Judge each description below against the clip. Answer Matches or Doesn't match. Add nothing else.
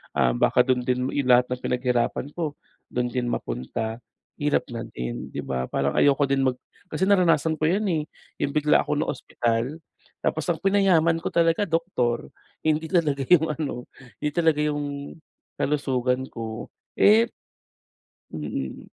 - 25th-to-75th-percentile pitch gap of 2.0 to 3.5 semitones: Doesn't match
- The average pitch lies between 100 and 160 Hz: Matches